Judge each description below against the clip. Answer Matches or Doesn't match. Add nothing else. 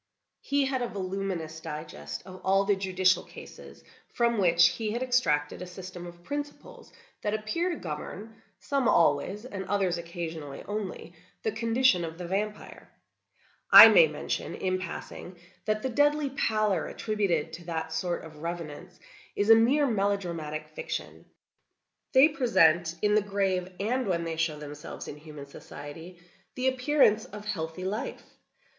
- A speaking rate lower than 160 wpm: Matches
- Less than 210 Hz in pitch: Matches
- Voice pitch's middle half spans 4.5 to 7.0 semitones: Matches